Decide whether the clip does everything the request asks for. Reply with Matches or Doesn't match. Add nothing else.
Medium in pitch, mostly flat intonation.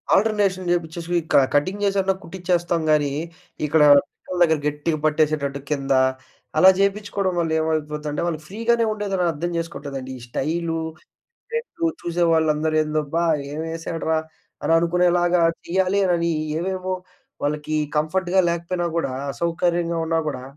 Doesn't match